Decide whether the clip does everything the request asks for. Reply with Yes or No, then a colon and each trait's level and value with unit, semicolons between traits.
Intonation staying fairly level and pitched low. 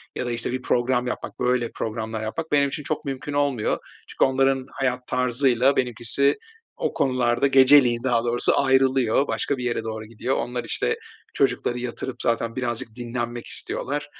Yes: narrow, 2.1 semitones; low, 125 Hz